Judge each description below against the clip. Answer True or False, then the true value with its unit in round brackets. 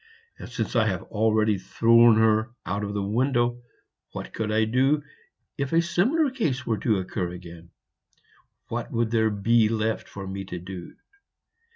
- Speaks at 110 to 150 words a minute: False (165 wpm)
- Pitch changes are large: False (3.2 semitones)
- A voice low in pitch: True (110 Hz)